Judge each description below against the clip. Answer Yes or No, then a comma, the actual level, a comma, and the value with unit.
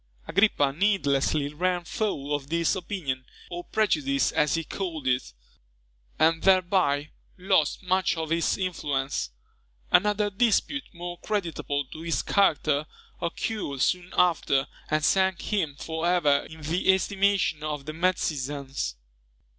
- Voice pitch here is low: No, medium, 165 Hz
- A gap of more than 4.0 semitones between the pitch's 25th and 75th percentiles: Yes, average, 4.5 semitones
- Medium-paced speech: No, slow, 125 wpm